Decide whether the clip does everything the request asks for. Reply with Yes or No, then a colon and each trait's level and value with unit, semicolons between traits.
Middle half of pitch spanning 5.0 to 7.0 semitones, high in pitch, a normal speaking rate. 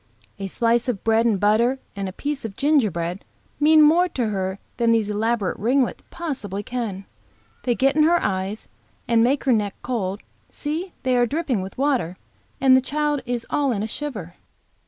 Yes: average, 5.3 semitones; high, 235 Hz; average, 180 wpm